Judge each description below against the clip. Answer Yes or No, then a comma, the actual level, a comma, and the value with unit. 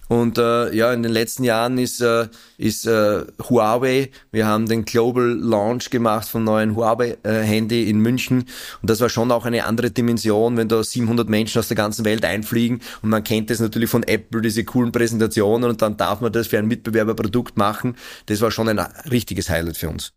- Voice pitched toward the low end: Yes, low, 115 Hz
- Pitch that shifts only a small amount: Yes, narrow, 1.5 semitones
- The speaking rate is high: Yes, fast, 205 wpm